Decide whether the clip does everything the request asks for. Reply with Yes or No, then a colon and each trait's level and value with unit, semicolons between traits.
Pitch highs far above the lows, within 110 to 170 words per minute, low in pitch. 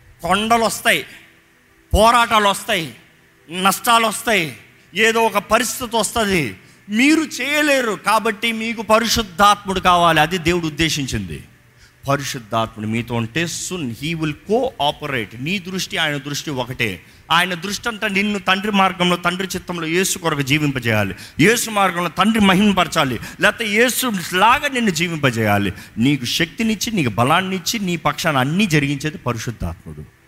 No: wide, 7.5 semitones; average, 120 wpm; medium, 180 Hz